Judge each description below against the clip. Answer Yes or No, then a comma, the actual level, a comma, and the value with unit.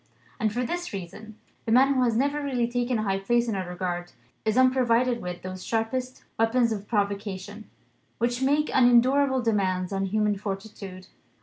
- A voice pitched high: Yes, high, 225 Hz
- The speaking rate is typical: Yes, average, 170 wpm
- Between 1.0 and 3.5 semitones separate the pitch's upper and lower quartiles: No, average, 4.2 semitones